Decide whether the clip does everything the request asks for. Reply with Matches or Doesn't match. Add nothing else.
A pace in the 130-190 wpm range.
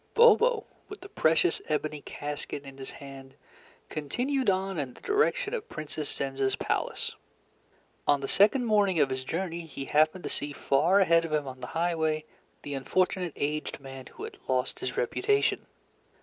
Matches